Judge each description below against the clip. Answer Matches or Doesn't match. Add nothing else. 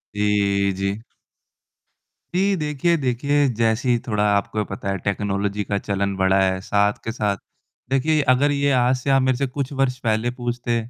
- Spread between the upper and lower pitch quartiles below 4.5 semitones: Doesn't match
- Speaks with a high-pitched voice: Doesn't match